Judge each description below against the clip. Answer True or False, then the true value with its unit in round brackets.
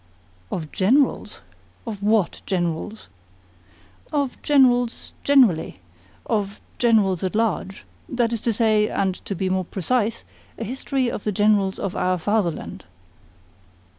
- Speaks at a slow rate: True (125 wpm)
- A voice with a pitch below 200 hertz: False (210 Hz)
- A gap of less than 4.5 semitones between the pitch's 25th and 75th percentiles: True (3.8 semitones)